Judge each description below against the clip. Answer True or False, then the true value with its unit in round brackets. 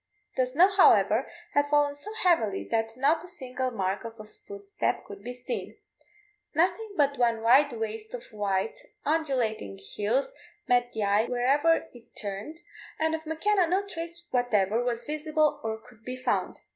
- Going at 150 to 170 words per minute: True (160 wpm)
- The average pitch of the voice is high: True (250 Hz)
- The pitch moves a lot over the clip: True (6.0 semitones)